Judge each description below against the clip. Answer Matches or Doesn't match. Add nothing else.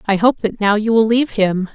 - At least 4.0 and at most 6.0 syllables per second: Matches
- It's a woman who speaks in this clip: Matches